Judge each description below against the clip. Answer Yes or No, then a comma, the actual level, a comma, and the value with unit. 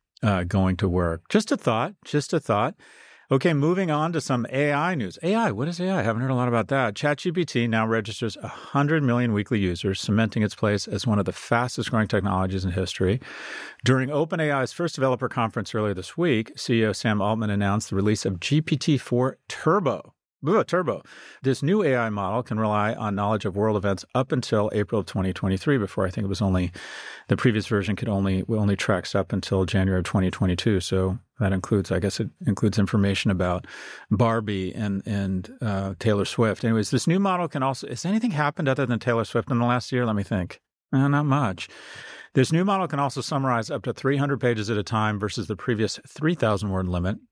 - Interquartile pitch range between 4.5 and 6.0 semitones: Yes, average, 5.1 semitones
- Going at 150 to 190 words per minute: No, average, 200 wpm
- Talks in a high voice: No, low, 115 Hz